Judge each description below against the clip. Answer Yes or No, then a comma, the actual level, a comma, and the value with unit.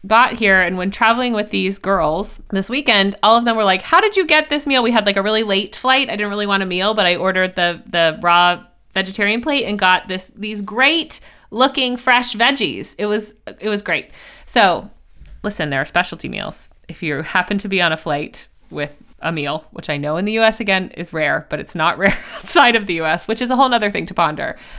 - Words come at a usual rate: No, fast, 235 wpm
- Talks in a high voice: Yes, high, 205 Hz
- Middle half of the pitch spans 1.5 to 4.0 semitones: No, average, 4.5 semitones